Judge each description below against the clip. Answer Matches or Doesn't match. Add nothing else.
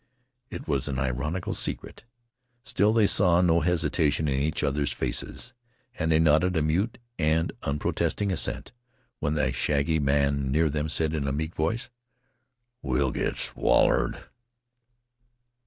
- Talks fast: Doesn't match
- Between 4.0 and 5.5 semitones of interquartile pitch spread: Doesn't match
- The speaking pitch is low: Matches